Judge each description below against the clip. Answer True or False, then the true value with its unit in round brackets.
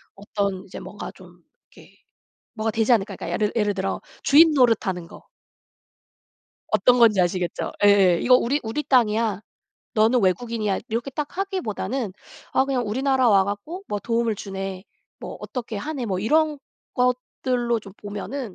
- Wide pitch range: False (4.0 semitones)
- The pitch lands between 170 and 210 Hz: False (225 Hz)